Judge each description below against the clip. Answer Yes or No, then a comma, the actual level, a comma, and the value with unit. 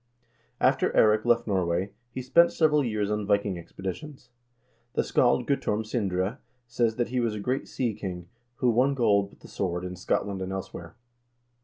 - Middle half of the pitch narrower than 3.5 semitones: No, average, 4.3 semitones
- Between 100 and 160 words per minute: No, average, 175 wpm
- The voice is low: Yes, low, 105 Hz